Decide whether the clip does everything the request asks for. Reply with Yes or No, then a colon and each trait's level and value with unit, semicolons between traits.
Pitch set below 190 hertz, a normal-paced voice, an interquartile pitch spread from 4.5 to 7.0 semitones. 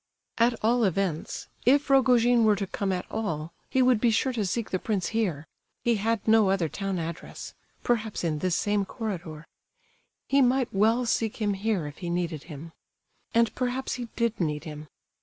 No: high, 210 Hz; average, 175 wpm; average, 5.1 semitones